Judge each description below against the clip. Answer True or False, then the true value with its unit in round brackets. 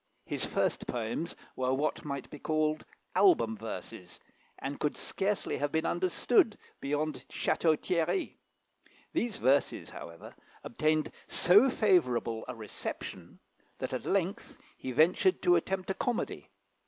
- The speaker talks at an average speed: False (130 wpm)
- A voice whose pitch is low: False (155 Hz)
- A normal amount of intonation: False (6.5 semitones)